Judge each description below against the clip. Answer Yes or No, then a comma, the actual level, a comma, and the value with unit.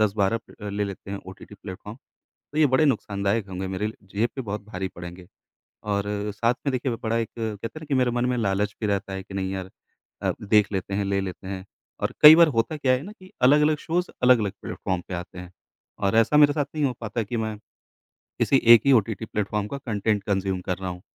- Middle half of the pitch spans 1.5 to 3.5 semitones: No, average, 4.2 semitones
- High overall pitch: No, low, 105 Hz